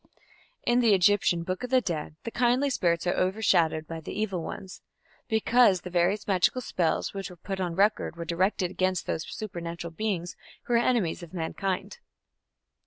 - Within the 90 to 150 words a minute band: No, average, 175 wpm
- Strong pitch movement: No, average, 4.1 semitones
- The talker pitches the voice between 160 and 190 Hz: Yes, medium, 185 Hz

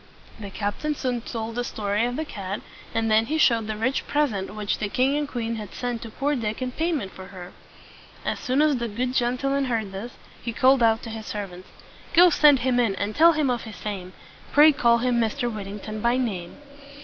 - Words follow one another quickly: Yes, fast, 215 wpm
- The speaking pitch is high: Yes, high, 235 Hz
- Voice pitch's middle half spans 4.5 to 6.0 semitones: No, average, 3.7 semitones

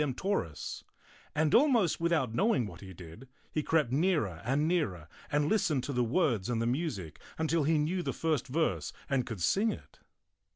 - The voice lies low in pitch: No, medium, 145 Hz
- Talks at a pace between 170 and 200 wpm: Yes, average, 180 wpm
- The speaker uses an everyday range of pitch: No, wide, 6.2 semitones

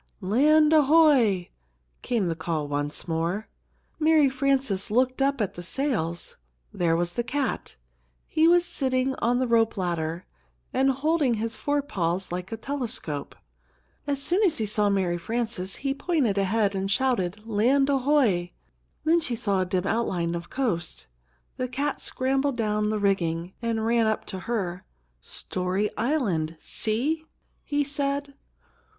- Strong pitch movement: Yes, wide, 6.8 semitones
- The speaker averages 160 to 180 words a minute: No, average, 145 wpm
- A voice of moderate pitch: No, high, 225 Hz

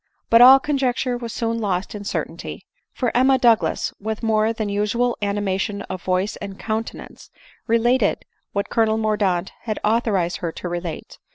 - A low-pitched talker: No, high, 215 Hz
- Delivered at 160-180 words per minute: Yes, average, 165 wpm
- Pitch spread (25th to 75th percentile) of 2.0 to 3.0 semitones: Yes, average, 2.7 semitones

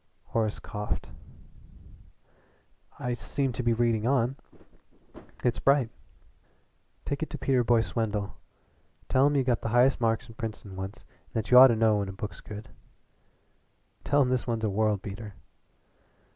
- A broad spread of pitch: No, average, 3.0 semitones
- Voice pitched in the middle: No, low, 115 Hz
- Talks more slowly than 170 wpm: Yes, average, 160 wpm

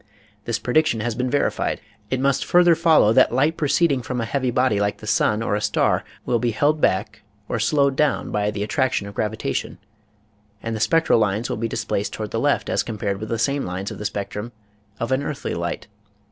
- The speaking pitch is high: No, low, 115 Hz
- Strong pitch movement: No, average, 4.7 semitones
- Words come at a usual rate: No, fast, 210 wpm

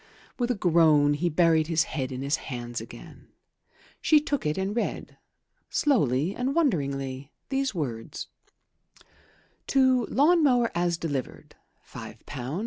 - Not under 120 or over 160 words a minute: Yes, slow, 135 wpm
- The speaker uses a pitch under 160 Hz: No, medium, 165 Hz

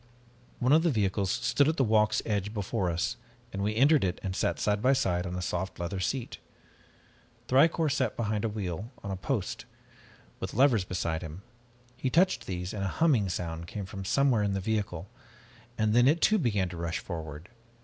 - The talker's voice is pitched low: Yes, low, 105 Hz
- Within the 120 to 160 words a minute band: No, average, 195 wpm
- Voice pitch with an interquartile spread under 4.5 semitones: No, average, 5.3 semitones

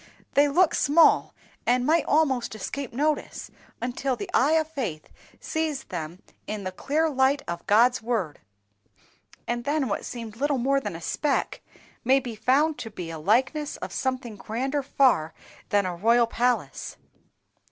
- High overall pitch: Yes, very high, 255 Hz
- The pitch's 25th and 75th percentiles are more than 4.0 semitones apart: Yes, average, 4.7 semitones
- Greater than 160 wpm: No, average, 155 wpm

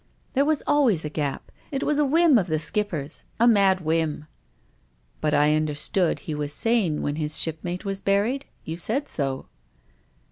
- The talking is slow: No, average, 190 wpm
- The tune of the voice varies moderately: No, wide, 7.2 semitones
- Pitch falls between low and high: Yes, medium, 175 Hz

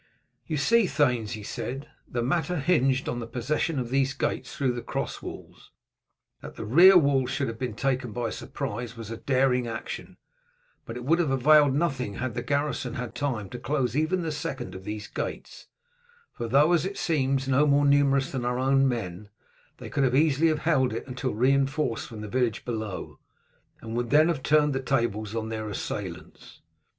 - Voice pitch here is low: Yes, low, 130 Hz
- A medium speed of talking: Yes, average, 185 wpm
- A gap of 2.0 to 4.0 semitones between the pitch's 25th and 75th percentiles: Yes, average, 3.5 semitones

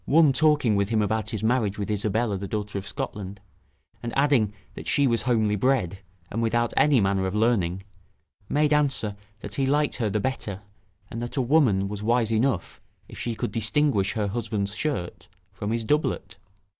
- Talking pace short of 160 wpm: No, average, 180 wpm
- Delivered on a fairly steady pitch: No, average, 4.3 semitones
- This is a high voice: No, low, 110 Hz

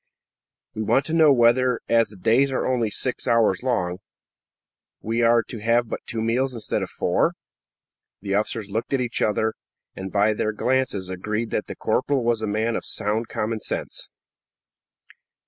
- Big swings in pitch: No, narrow, 2.5 semitones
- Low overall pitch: Yes, low, 115 Hz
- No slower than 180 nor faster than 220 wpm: No, average, 170 wpm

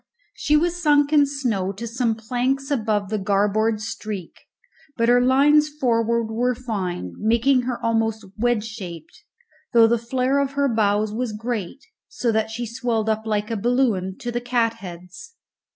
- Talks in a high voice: Yes, high, 230 Hz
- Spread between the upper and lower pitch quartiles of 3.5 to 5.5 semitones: No, average, 2.9 semitones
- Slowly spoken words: No, average, 160 wpm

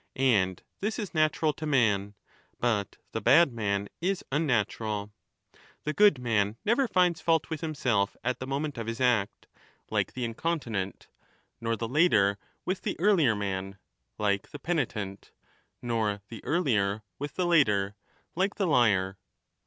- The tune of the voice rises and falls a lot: Yes, wide, 7.3 semitones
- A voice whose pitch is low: Yes, low, 120 Hz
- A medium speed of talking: Yes, average, 145 wpm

